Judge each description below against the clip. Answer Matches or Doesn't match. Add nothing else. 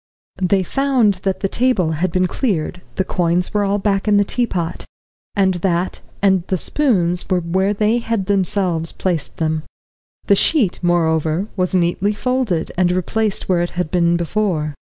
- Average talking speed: Matches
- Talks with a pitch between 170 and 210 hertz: Matches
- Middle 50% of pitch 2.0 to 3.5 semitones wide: Matches